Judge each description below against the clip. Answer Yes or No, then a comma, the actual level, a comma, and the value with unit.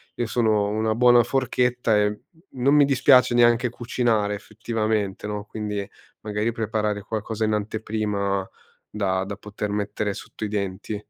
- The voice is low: Yes, low, 110 Hz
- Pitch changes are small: Yes, narrow, 2.3 semitones